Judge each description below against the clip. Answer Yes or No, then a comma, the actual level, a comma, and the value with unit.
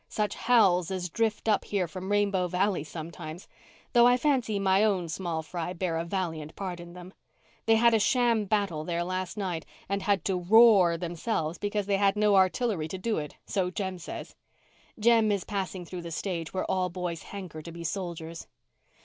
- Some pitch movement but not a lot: Yes, average, 3.2 semitones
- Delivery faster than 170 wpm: Yes, average, 190 wpm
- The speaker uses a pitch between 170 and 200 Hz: Yes, medium, 185 Hz